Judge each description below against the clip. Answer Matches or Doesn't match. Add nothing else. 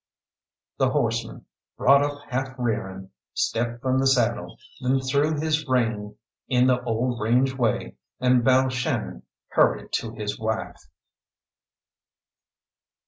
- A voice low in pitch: Matches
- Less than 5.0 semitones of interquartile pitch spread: Matches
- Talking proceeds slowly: Matches